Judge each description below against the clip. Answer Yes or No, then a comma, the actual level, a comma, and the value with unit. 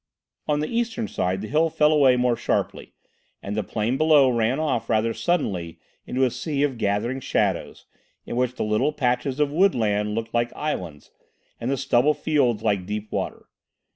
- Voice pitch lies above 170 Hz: No, low, 125 Hz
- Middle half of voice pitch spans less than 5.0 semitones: No, wide, 5.4 semitones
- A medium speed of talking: Yes, average, 175 wpm